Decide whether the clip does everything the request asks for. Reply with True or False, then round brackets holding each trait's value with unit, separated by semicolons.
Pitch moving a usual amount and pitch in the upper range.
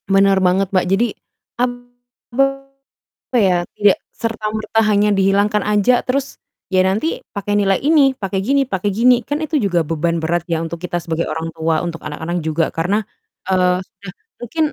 False (5.8 semitones; 200 Hz)